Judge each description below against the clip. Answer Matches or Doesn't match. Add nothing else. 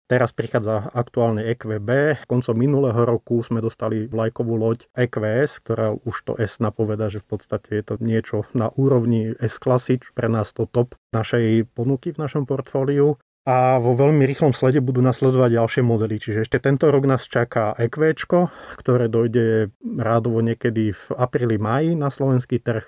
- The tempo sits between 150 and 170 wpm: Matches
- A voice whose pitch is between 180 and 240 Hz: Doesn't match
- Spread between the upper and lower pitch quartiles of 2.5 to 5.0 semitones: Matches